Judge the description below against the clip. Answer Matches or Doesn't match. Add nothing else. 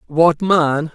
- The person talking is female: Doesn't match